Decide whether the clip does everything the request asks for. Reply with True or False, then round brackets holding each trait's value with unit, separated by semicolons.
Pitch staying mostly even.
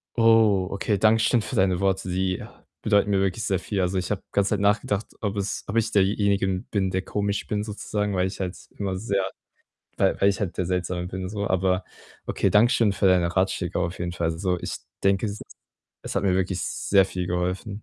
True (1.8 semitones)